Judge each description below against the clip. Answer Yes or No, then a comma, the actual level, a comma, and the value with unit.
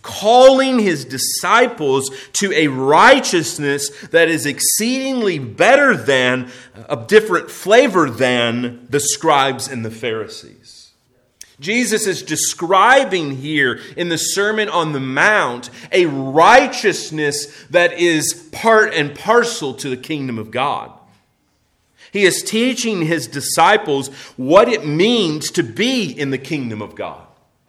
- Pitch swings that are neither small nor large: No, wide, 7.1 semitones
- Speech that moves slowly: Yes, slow, 125 wpm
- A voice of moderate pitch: Yes, medium, 155 Hz